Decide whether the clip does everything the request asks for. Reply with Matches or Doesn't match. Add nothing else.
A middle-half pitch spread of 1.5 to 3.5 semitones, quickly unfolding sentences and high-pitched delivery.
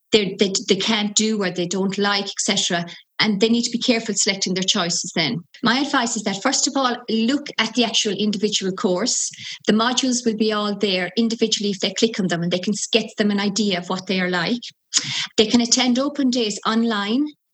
Matches